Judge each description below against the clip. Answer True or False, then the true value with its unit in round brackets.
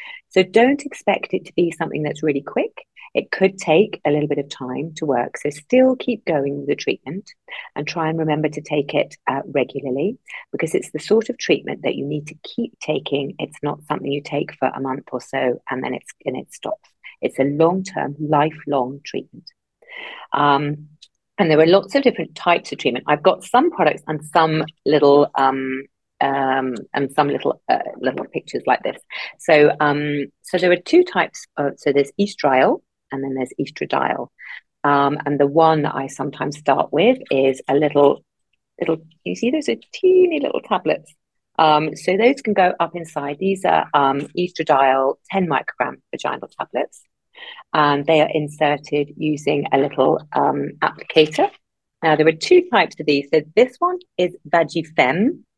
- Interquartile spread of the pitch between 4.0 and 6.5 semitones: True (4.6 semitones)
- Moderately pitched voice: True (155 Hz)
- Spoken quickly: False (180 wpm)